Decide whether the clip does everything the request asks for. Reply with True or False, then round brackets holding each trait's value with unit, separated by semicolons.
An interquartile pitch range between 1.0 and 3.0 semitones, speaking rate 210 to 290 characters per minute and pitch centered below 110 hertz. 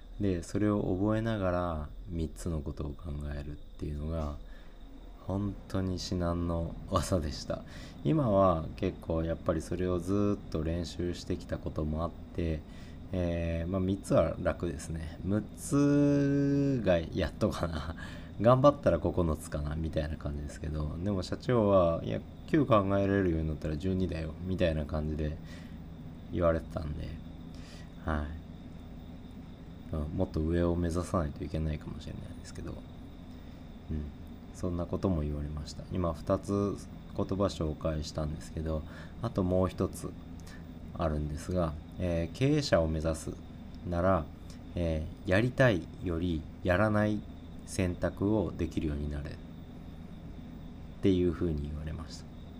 True (2.5 semitones; 265 characters per minute; 85 Hz)